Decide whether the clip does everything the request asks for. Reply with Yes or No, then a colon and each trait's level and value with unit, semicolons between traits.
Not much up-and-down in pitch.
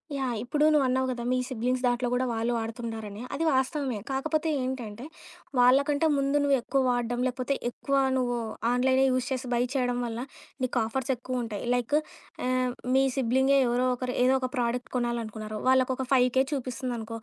Yes: narrow, 1.7 semitones